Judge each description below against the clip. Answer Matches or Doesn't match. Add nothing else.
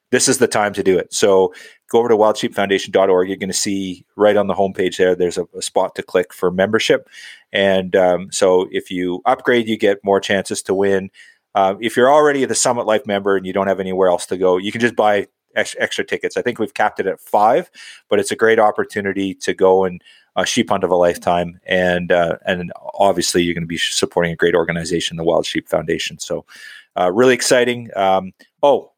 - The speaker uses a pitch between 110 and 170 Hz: Doesn't match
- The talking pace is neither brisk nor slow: Doesn't match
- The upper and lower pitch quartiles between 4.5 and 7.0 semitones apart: Doesn't match